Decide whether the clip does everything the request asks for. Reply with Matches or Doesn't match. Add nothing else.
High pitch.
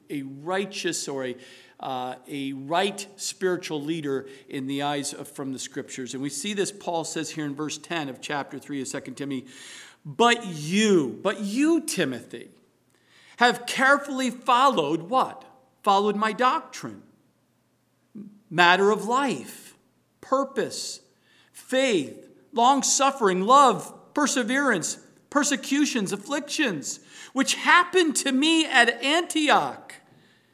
Matches